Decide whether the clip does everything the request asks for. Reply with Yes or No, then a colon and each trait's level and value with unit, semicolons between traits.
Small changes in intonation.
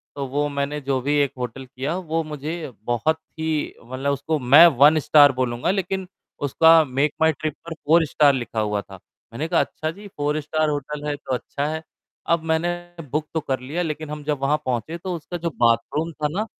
No: average, 3.0 semitones